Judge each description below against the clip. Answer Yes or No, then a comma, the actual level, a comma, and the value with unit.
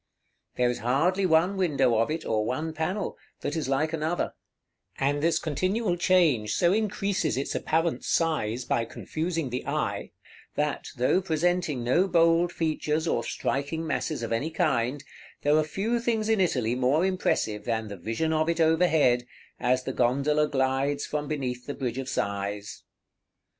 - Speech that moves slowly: No, average, 160 wpm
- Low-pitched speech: No, medium, 150 Hz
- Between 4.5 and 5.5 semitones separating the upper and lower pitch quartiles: Yes, average, 5.0 semitones